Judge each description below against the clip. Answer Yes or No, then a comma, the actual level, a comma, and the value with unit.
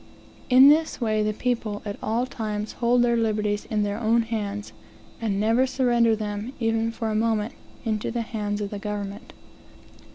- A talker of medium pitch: No, high, 220 Hz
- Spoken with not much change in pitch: Yes, narrow, 2.1 semitones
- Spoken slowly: No, average, 170 wpm